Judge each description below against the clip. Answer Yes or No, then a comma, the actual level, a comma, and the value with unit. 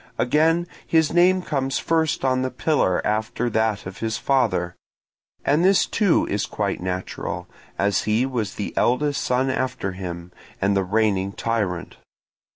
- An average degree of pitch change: No, wide, 6.3 semitones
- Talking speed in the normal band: Yes, average, 145 wpm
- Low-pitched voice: Yes, low, 115 Hz